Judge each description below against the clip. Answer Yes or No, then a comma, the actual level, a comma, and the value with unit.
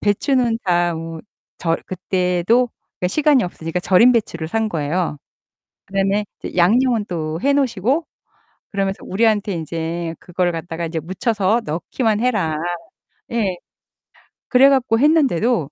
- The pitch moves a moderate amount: No, wide, 5.7 semitones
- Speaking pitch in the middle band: No, high, 195 Hz